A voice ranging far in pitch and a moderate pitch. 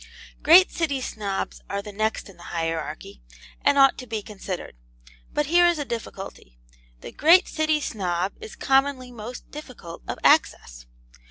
No: wide, 7.9 semitones; high, 230 Hz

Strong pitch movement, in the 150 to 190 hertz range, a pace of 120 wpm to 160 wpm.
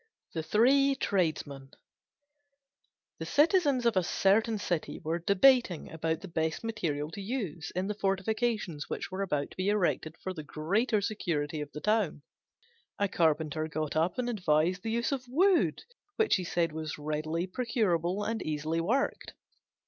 Yes: wide, 6.0 semitones; medium, 185 Hz; average, 155 wpm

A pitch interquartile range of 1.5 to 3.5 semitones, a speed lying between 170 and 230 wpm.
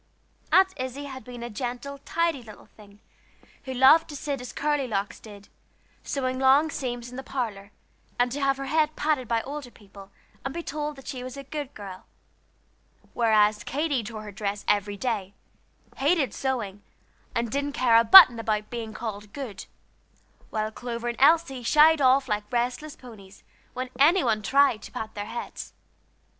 No: average, 4.4 semitones; average, 175 wpm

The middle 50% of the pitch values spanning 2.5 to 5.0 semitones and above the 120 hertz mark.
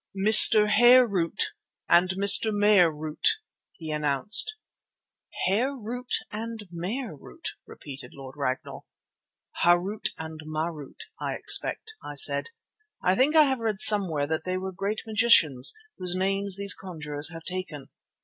No: wide, 5.5 semitones; medium, 185 Hz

